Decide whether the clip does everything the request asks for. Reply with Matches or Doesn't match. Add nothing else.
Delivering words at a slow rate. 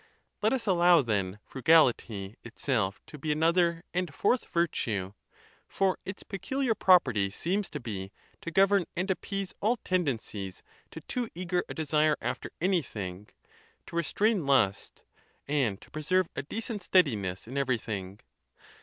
Doesn't match